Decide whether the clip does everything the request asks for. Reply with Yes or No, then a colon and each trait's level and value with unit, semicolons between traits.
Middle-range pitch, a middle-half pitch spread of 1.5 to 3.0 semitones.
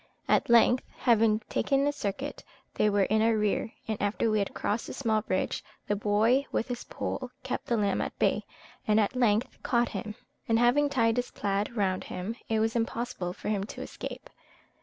No: high, 220 Hz; narrow, 2.6 semitones